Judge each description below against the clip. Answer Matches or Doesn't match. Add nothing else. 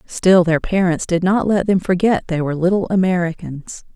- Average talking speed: Matches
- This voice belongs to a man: Doesn't match